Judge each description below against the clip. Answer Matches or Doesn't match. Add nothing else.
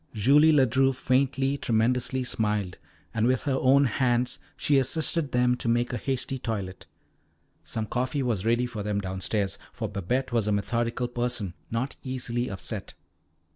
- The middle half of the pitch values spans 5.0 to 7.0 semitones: Doesn't match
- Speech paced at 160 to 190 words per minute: Doesn't match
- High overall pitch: Doesn't match